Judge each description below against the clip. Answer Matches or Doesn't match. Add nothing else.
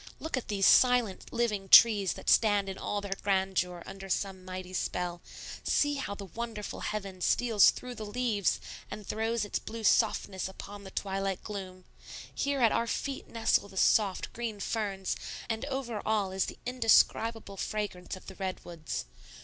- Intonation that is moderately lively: Matches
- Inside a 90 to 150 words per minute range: Doesn't match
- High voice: Matches